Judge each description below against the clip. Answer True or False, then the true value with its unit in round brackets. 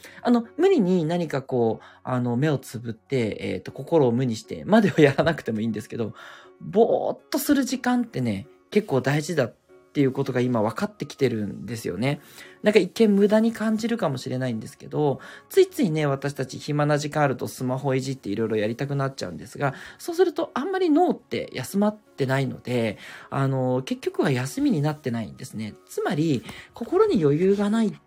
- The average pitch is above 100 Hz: True (140 Hz)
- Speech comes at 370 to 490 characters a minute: True (400 characters per minute)